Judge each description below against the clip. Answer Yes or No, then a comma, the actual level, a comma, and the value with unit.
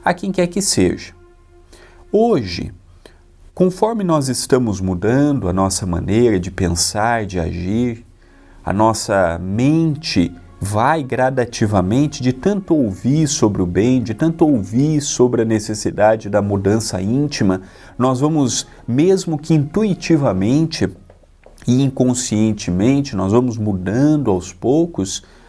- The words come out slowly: Yes, slow, 115 wpm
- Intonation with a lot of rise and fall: Yes, wide, 7.1 semitones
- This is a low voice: Yes, low, 110 Hz